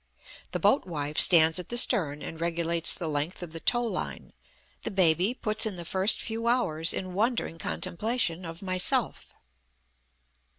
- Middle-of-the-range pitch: Yes, medium, 180 Hz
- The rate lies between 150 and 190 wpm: Yes, average, 160 wpm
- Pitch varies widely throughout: No, average, 4.7 semitones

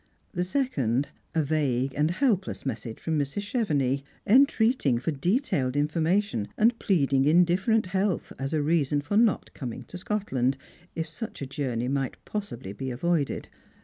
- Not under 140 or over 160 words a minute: Yes, average, 145 wpm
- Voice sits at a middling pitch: Yes, medium, 155 Hz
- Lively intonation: Yes, wide, 6.7 semitones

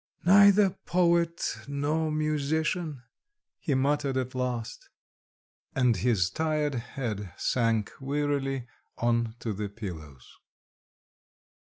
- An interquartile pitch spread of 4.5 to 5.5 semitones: Yes, average, 4.8 semitones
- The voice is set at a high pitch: No, low, 135 Hz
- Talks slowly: Yes, slow, 90 wpm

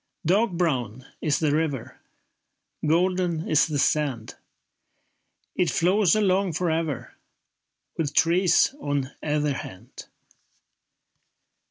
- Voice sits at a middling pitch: Yes, medium, 160 Hz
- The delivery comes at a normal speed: No, slow, 95 wpm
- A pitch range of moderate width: Yes, average, 3.9 semitones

